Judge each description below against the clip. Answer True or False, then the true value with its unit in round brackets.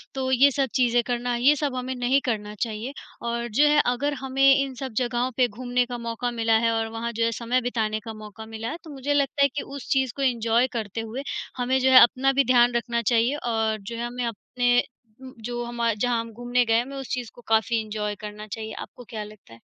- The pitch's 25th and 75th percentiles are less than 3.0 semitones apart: True (2.4 semitones)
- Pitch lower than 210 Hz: False (240 Hz)